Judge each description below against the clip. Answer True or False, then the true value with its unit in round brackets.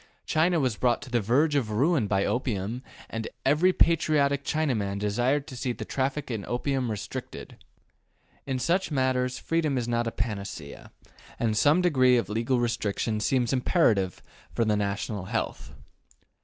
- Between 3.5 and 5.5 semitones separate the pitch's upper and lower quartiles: True (4.6 semitones)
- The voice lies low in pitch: True (125 Hz)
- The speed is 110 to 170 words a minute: True (155 wpm)